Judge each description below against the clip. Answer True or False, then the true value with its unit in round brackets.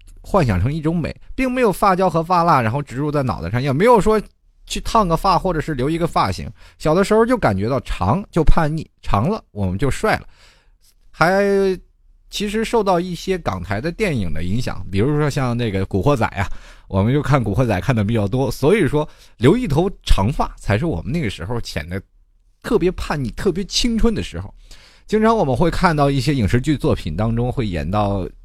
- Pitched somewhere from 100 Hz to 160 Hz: True (135 Hz)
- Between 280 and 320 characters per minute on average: True (300 characters per minute)